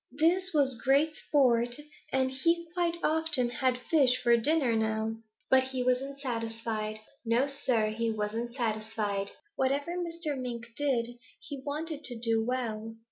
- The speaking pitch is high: Yes, very high, 255 Hz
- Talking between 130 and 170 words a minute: Yes, average, 140 wpm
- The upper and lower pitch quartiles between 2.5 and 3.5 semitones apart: No, average, 4.0 semitones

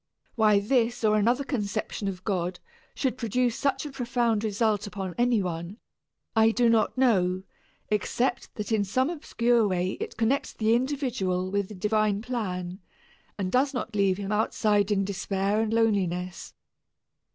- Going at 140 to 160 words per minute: Yes, average, 150 wpm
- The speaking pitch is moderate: No, high, 215 Hz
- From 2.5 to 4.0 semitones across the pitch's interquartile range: Yes, average, 3.6 semitones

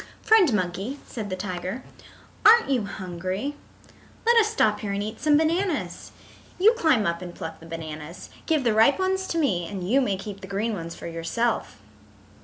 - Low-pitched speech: No, high, 210 Hz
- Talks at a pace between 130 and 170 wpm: No, average, 185 wpm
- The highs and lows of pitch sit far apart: Yes, wide, 8.4 semitones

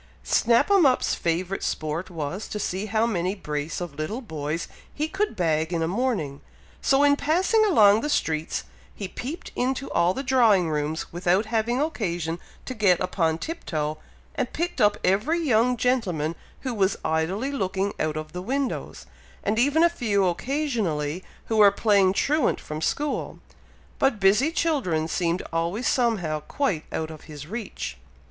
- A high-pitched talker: Yes, high, 200 Hz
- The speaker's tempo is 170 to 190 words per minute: No, average, 160 wpm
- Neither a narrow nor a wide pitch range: No, wide, 7.6 semitones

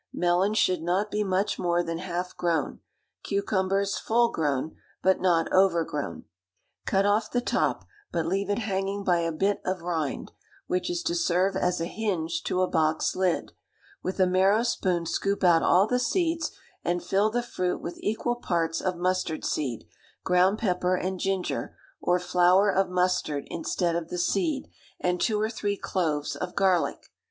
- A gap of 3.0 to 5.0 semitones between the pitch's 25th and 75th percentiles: No, narrow, 2.6 semitones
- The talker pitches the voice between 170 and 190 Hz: Yes, medium, 185 Hz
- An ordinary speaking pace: Yes, average, 170 wpm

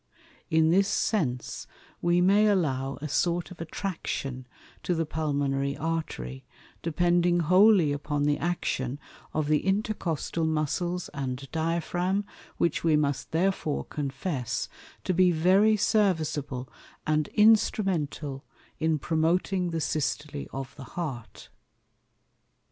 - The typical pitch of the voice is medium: Yes, medium, 160 Hz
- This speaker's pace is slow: Yes, slow, 115 wpm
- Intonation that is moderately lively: Yes, average, 3.9 semitones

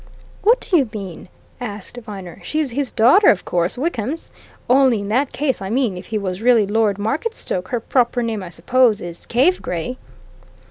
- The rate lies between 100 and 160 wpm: No, average, 180 wpm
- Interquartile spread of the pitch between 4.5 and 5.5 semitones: Yes, average, 4.8 semitones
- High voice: Yes, high, 230 Hz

